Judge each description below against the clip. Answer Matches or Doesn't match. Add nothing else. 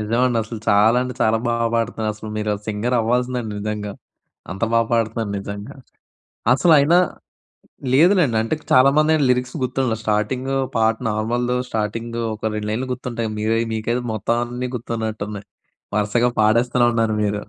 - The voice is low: Matches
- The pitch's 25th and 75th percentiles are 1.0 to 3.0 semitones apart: Matches